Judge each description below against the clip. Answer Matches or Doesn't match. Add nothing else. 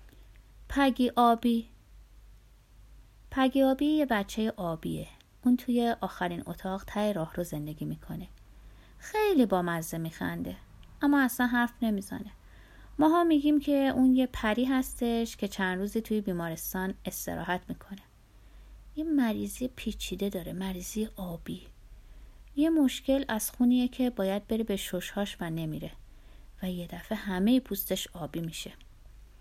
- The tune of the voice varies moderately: Doesn't match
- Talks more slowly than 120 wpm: Doesn't match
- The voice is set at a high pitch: Matches